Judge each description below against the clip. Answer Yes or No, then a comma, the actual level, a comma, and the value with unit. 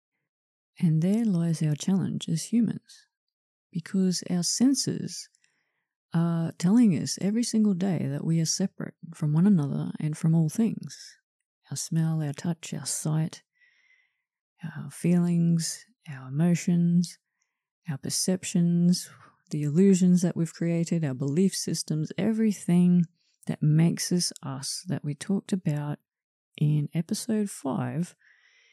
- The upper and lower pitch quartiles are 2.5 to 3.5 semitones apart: No, average, 4.0 semitones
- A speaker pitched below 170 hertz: No, medium, 175 Hz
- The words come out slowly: Yes, slow, 125 wpm